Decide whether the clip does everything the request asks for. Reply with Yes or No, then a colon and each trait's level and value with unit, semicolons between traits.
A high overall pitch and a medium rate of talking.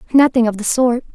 No: high, 240 Hz; fast, 210 wpm